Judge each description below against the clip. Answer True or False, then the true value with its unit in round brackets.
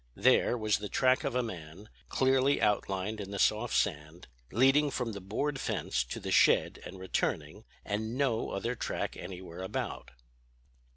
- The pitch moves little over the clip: False (5.1 semitones)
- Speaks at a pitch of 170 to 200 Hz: False (105 Hz)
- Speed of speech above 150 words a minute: True (160 wpm)